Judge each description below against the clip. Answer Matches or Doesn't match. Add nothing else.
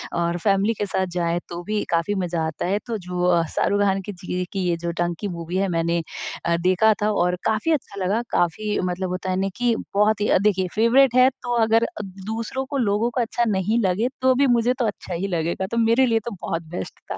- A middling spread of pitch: Matches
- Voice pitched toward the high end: Matches